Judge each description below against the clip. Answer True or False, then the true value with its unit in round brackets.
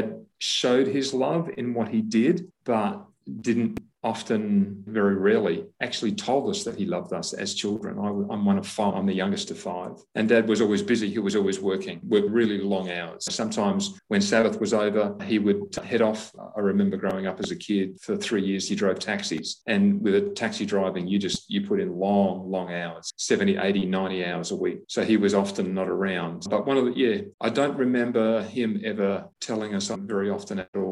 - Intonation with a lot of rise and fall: True (5.8 semitones)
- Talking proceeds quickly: True (210 wpm)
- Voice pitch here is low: True (110 Hz)